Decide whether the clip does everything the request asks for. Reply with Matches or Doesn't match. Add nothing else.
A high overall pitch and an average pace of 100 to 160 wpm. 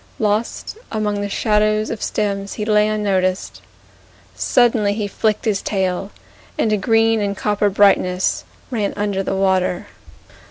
Matches